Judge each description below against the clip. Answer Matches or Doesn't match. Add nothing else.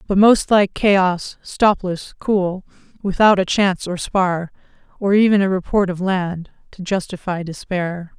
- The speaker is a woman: Matches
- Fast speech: Doesn't match